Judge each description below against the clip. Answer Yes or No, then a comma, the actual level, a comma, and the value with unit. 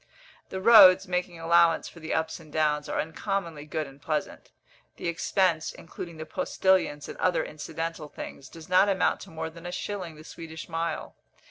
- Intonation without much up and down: Yes, narrow, 2.3 semitones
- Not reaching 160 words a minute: No, average, 175 wpm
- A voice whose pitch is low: No, medium, 165 Hz